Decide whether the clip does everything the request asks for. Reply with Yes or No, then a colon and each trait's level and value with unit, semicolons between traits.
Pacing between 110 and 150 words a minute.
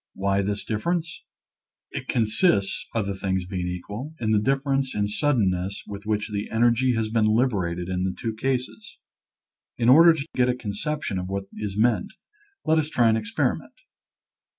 No: average, 165 wpm